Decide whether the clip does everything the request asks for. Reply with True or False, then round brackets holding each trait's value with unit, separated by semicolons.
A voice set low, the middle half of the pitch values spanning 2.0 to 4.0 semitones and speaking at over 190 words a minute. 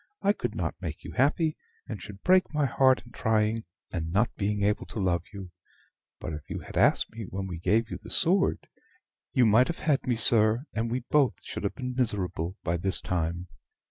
False (110 Hz; 5.3 semitones; 205 wpm)